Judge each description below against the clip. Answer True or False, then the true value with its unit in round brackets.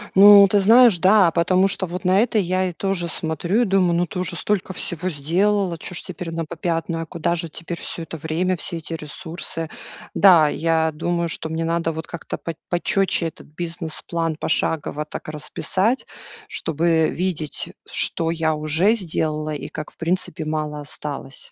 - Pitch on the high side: False (170 Hz)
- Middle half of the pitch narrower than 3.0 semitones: True (2.6 semitones)